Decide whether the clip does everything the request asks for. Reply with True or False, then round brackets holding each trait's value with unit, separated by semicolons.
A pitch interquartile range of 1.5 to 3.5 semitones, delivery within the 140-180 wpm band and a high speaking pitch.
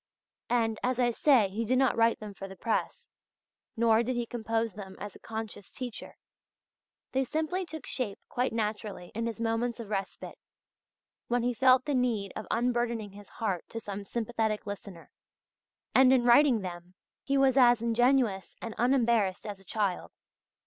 True (3.1 semitones; 170 wpm; 230 Hz)